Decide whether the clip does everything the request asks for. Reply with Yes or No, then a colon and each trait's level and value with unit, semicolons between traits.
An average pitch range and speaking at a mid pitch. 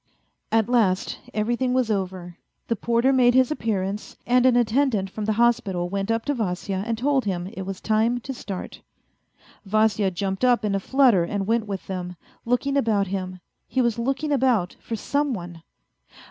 No: average, 4.2 semitones; high, 220 Hz